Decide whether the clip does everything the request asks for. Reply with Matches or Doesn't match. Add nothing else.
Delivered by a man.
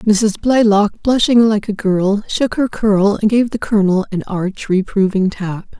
Doesn't match